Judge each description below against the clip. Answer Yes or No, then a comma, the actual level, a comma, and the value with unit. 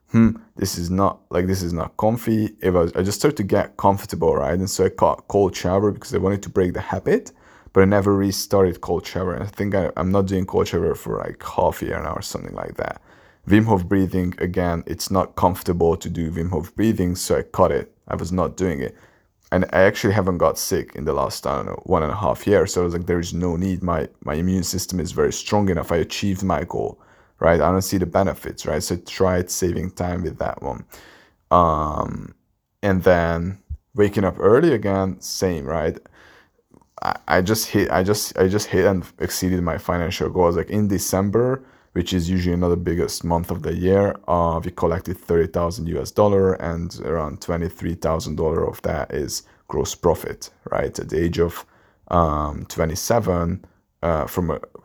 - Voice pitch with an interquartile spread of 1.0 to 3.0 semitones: Yes, narrow, 2.6 semitones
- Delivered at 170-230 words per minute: Yes, fast, 205 wpm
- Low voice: Yes, very low, 90 Hz